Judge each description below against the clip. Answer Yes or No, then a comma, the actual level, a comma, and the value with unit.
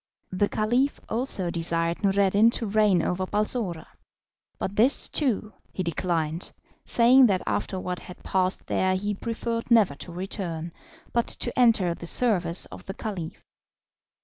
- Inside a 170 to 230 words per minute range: No, average, 145 wpm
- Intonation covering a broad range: No, average, 4.5 semitones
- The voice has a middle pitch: No, high, 195 Hz